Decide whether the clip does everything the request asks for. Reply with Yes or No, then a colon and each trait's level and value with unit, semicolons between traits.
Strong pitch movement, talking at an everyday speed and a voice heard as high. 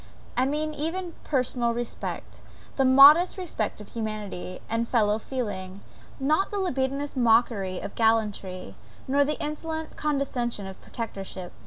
No: wide, 5.8 semitones; slow, 130 wpm; high, 245 Hz